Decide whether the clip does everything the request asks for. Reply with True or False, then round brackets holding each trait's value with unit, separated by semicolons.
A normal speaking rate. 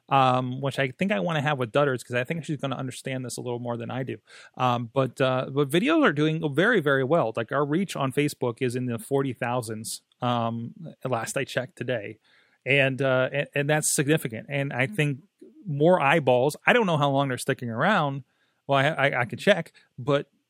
False (220 wpm)